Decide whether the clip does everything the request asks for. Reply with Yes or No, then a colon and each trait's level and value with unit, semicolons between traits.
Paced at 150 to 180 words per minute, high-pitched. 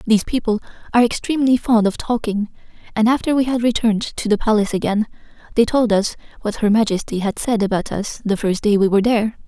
No: fast, 205 wpm; high, 220 Hz